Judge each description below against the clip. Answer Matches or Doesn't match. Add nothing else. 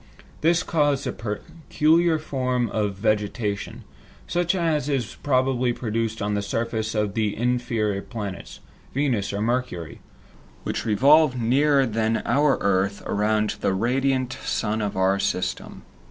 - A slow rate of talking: Matches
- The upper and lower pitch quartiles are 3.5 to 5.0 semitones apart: Matches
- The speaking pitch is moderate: Doesn't match